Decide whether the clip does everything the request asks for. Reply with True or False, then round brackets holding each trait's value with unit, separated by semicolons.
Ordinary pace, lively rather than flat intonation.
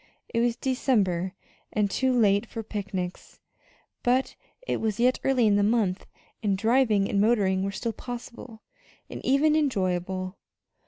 False (145 wpm; 4.0 semitones)